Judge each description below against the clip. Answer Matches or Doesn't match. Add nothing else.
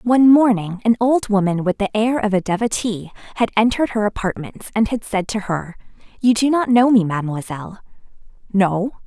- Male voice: Doesn't match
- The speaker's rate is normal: Matches